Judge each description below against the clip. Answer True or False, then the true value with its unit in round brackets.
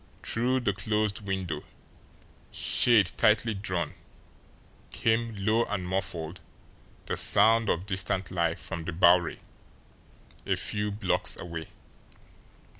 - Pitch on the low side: True (95 Hz)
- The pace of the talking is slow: True (110 wpm)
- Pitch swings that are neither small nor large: True (3.7 semitones)